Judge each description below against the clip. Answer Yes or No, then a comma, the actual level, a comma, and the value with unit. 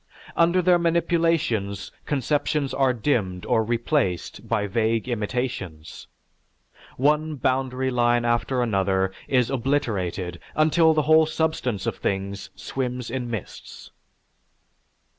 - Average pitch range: No, wide, 6.4 semitones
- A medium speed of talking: No, slow, 105 wpm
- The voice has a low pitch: Yes, low, 125 Hz